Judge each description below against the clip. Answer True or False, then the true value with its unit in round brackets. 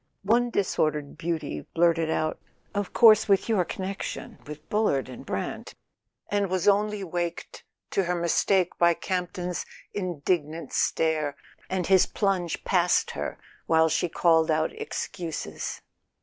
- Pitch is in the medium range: True (175 Hz)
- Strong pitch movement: False (3.4 semitones)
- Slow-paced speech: True (125 wpm)